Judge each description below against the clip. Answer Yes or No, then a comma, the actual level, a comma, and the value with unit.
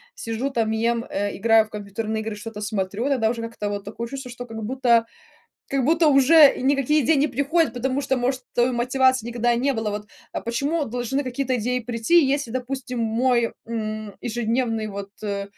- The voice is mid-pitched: No, high, 240 Hz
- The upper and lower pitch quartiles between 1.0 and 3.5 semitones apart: Yes, average, 3.2 semitones